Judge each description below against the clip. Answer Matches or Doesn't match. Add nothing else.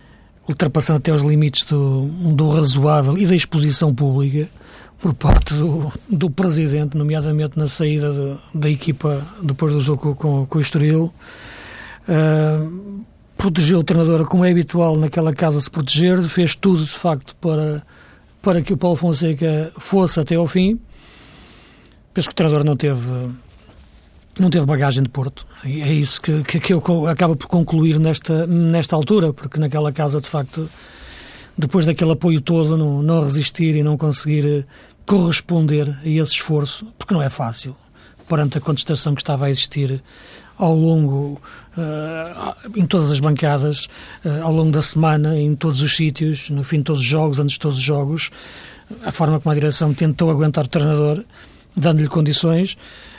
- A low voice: Doesn't match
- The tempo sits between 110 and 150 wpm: Doesn't match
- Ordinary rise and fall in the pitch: Doesn't match